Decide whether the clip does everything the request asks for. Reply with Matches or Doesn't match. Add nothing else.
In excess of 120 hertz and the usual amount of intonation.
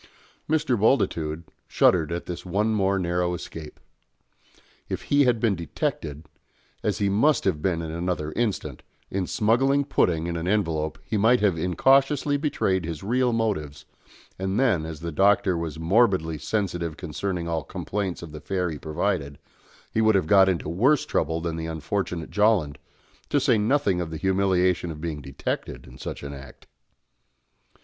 Doesn't match